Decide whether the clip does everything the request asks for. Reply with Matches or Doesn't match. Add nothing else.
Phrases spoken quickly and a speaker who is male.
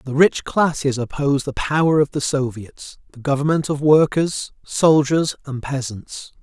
Doesn't match